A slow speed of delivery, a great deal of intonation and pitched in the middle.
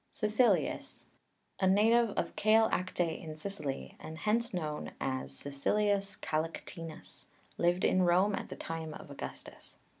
No: slow, 130 wpm; average, 5.0 semitones; medium, 180 Hz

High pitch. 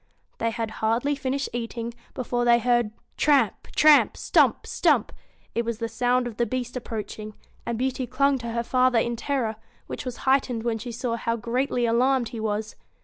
Yes: high, 240 Hz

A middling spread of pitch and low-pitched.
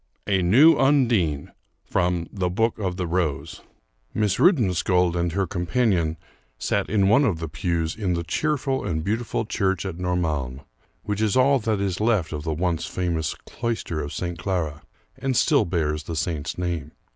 Yes: average, 4.6 semitones; very low, 90 Hz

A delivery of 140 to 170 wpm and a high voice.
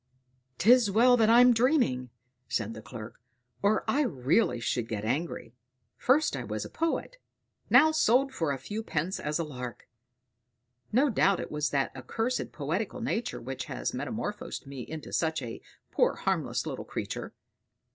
No: average, 155 wpm; medium, 170 Hz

